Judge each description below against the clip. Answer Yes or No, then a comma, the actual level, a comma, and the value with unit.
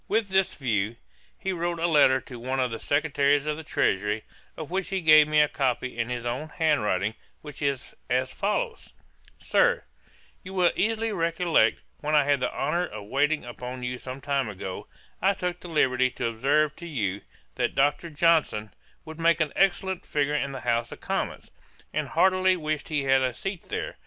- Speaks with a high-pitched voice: No, medium, 145 Hz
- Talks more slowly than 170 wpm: No, average, 190 wpm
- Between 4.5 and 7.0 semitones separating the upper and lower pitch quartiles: Yes, average, 5.0 semitones